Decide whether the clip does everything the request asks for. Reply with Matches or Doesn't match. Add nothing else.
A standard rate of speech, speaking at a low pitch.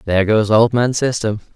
Matches